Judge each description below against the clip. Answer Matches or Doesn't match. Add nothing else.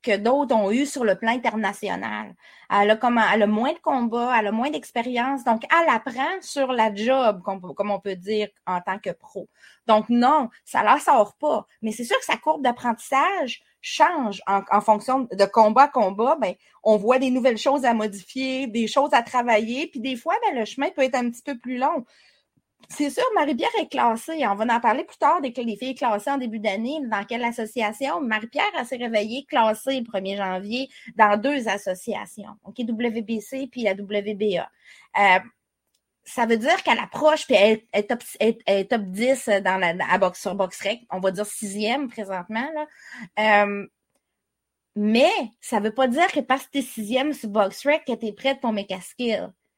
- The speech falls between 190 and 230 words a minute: Matches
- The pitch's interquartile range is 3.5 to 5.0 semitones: Matches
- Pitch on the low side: Doesn't match